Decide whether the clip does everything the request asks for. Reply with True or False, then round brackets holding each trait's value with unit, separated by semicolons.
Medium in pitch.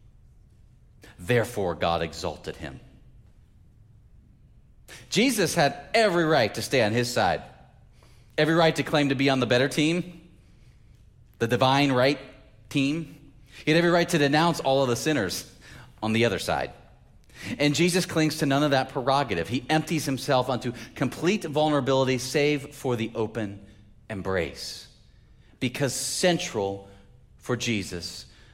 False (130 Hz)